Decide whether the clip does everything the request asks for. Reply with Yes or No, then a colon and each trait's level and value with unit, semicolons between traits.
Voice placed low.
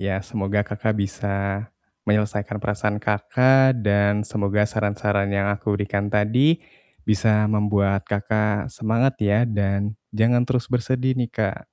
Yes: low, 105 Hz